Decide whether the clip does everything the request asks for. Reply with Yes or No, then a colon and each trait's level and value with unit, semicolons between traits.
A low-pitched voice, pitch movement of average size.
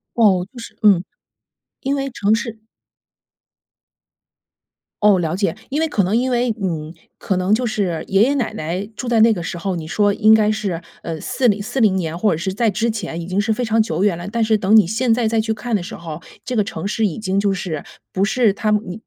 No: high, 210 Hz; average, 3.6 semitones